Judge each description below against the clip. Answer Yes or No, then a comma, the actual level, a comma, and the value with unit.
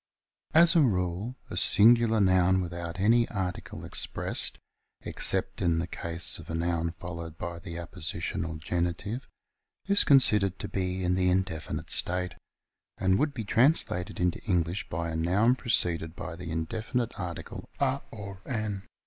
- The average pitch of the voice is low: Yes, very low, 90 Hz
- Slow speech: No, average, 155 wpm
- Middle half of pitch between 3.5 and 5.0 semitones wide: Yes, average, 4.2 semitones